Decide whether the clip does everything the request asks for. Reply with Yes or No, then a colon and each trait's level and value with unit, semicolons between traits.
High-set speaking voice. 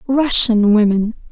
Yes: high, 225 Hz